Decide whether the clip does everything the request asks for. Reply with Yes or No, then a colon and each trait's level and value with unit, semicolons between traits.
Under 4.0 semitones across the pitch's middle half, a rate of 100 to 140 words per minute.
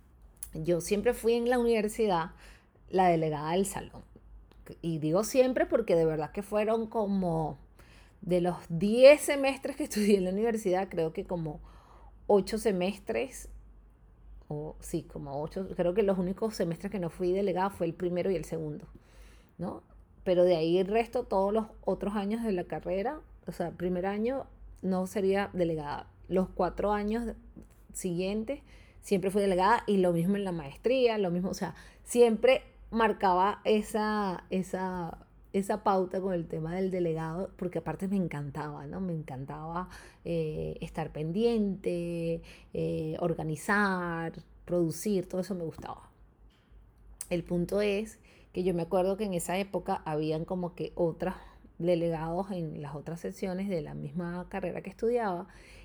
No: average, 3.6 semitones; average, 155 wpm